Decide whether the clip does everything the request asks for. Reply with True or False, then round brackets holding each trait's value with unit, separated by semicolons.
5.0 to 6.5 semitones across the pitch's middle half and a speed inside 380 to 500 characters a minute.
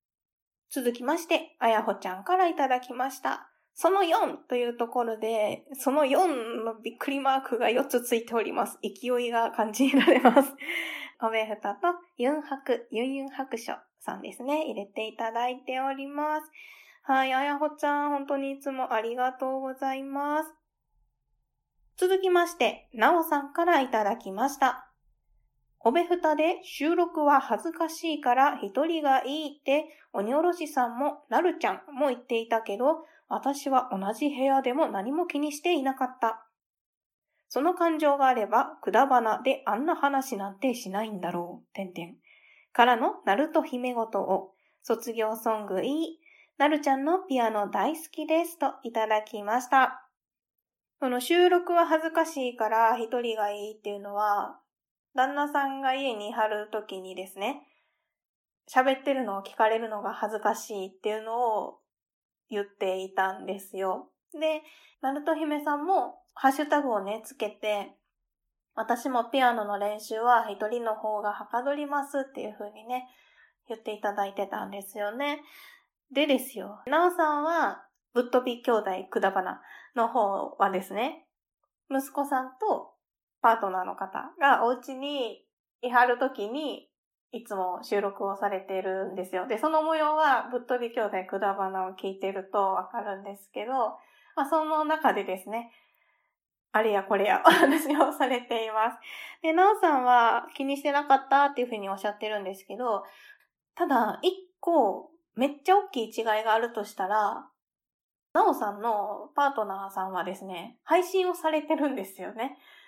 False (5.6 semitones; 310 characters per minute)